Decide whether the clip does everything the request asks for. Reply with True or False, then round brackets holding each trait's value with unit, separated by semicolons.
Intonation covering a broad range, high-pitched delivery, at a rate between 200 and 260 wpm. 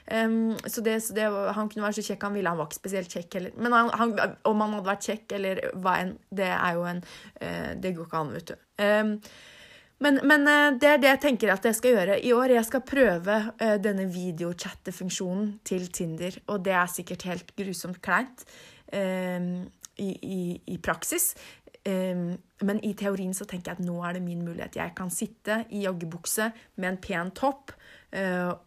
False (3.5 semitones; 195 Hz; 205 wpm)